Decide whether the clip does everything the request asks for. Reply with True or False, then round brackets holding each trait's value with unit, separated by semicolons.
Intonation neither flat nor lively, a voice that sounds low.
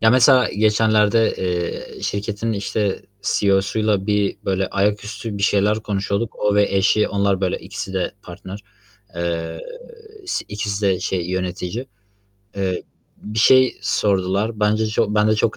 False (1.9 semitones; 105 Hz)